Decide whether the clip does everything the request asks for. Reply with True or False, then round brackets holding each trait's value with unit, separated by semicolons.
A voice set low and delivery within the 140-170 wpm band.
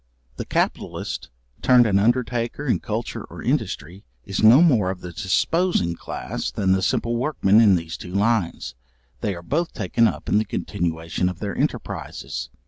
True (105 Hz; 165 wpm)